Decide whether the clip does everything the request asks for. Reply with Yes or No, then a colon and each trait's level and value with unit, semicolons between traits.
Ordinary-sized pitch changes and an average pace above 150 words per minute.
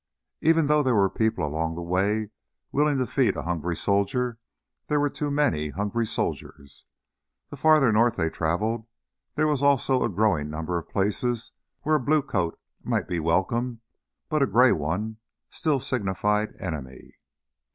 No: wide, 7.3 semitones; average, 160 wpm